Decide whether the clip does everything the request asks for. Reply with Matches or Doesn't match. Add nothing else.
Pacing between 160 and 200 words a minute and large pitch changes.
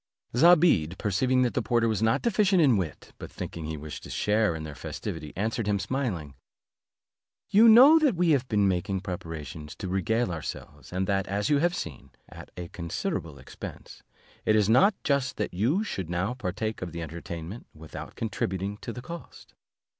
Matches